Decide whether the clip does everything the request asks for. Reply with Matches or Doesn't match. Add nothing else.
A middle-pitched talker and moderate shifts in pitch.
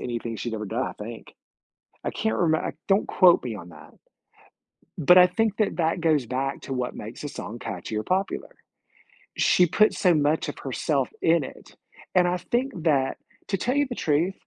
Doesn't match